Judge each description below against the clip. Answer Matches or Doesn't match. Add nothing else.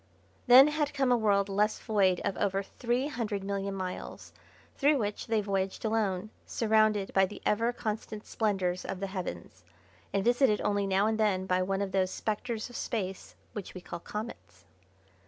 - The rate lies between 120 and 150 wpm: Doesn't match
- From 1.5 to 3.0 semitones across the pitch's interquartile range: Matches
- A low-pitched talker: Doesn't match